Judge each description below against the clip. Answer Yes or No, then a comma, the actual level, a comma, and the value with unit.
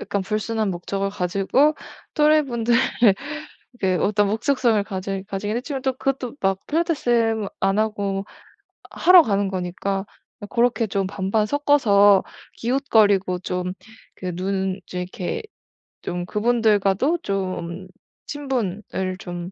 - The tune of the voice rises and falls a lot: No, average, 3.9 semitones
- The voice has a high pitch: Yes, high, 205 Hz